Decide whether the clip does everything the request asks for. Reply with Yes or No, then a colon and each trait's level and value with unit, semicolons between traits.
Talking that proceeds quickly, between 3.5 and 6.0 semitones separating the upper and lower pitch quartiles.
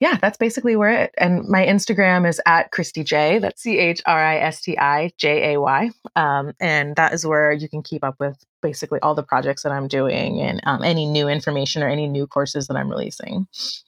No: average, 185 wpm; average, 4.1 semitones